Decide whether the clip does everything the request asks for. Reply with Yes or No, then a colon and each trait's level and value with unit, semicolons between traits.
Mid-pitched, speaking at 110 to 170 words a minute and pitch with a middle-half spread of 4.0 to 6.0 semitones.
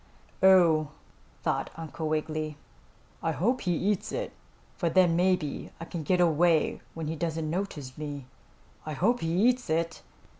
No: medium, 165 Hz; average, 150 wpm; average, 3.0 semitones